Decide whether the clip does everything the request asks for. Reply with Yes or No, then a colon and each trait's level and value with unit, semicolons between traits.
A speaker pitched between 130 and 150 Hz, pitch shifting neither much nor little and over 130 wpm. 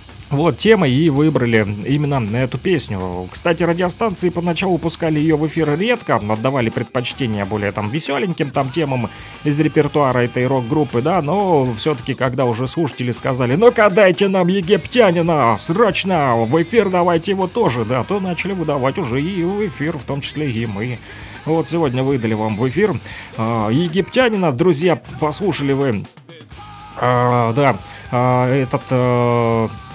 No: medium, 140 Hz; wide, 6.0 semitones; average, 140 wpm